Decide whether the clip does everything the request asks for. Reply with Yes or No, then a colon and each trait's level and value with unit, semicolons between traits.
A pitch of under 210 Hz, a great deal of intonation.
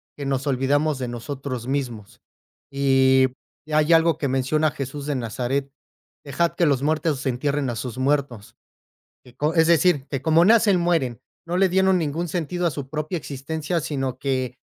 No: medium, 140 Hz; average, 3.4 semitones